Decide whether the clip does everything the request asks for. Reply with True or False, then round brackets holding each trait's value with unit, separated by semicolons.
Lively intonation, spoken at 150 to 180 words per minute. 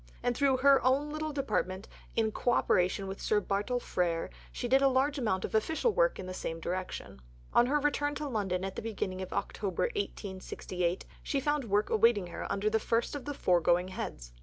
False (6.7 semitones; 200 wpm)